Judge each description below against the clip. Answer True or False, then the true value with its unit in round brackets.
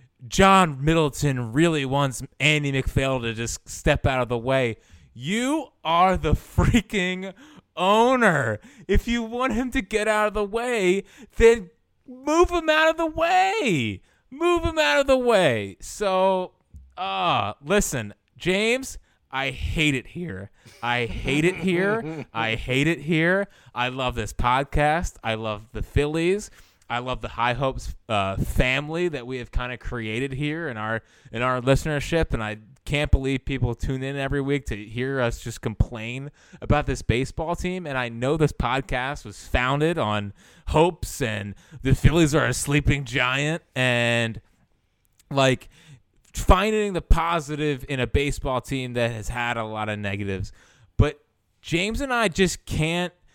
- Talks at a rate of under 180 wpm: True (155 wpm)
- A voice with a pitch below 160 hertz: True (140 Hz)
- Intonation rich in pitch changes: True (7.1 semitones)